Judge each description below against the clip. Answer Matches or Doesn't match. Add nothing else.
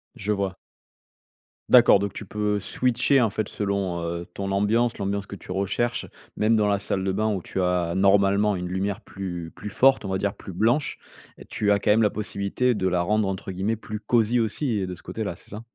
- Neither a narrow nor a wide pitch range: Doesn't match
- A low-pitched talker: Matches